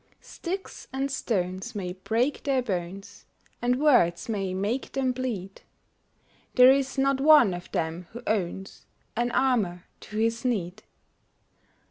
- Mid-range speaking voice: No, high, 225 Hz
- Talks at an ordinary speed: No, slow, 130 wpm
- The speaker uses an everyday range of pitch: No, wide, 5.9 semitones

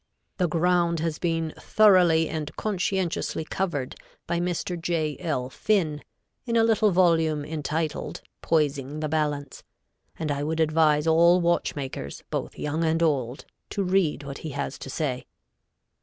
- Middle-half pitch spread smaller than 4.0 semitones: Yes, average, 2.7 semitones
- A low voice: No, medium, 160 Hz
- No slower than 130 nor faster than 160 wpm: Yes, average, 140 wpm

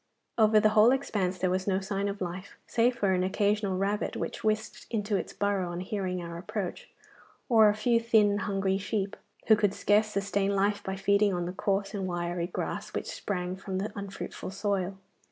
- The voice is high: Yes, high, 200 Hz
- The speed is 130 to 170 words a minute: No, average, 195 wpm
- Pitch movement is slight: Yes, narrow, 2.0 semitones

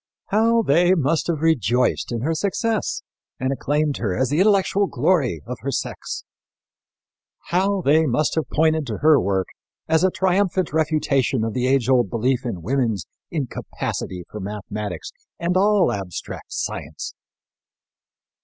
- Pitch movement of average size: No, wide, 6.7 semitones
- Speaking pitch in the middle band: Yes, medium, 145 Hz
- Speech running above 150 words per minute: No, average, 145 wpm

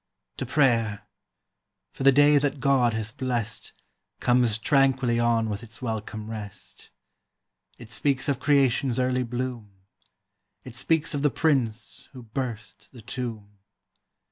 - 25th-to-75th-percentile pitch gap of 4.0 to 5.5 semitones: No, average, 3.3 semitones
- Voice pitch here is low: Yes, low, 120 Hz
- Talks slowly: Yes, slow, 130 wpm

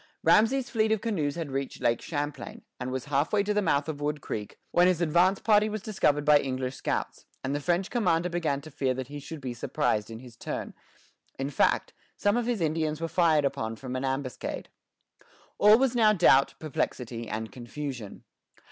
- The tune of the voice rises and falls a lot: Yes, wide, 5.9 semitones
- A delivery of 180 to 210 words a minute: Yes, average, 190 wpm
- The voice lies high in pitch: No, medium, 150 Hz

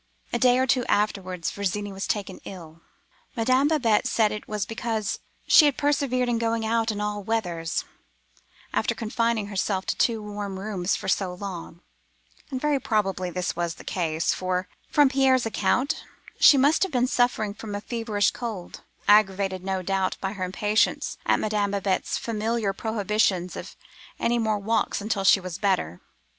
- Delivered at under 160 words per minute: No, average, 170 wpm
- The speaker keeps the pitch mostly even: No, average, 3.4 semitones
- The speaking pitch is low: No, high, 210 Hz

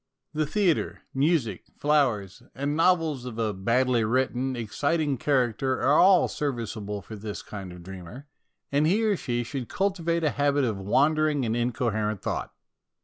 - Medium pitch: No, low, 130 Hz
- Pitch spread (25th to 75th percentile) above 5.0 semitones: Yes, wide, 5.5 semitones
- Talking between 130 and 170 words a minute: Yes, average, 150 wpm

